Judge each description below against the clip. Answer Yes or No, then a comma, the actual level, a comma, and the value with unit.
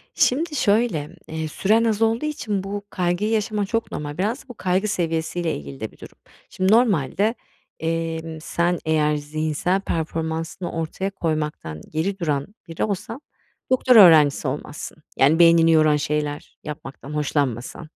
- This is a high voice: No, medium, 165 Hz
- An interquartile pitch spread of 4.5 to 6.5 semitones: Yes, average, 5.0 semitones